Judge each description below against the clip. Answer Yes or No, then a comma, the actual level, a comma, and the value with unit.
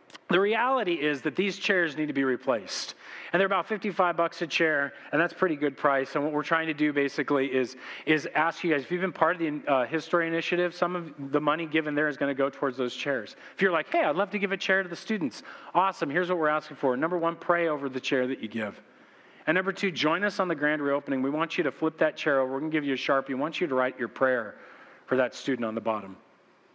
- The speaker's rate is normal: No, fast, 270 wpm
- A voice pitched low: No, medium, 155 Hz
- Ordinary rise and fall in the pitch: Yes, average, 4.3 semitones